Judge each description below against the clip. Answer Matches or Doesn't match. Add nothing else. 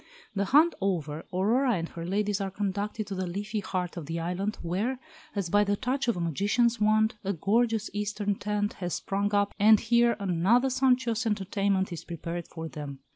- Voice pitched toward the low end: Doesn't match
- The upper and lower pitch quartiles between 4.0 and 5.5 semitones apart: Doesn't match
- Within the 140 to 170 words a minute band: Doesn't match